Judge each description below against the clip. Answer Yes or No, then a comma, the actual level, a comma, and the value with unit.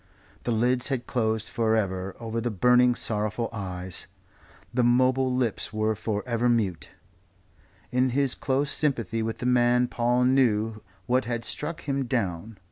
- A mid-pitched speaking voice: No, low, 120 Hz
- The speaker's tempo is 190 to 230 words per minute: No, average, 150 wpm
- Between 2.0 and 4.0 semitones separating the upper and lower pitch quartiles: Yes, narrow, 2.5 semitones